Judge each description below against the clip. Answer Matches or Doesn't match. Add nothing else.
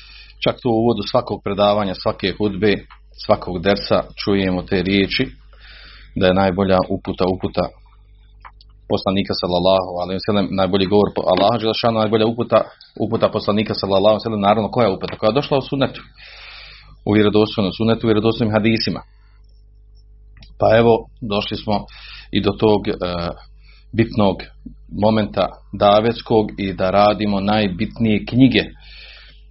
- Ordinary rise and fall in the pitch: Doesn't match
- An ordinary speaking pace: Matches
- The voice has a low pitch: Matches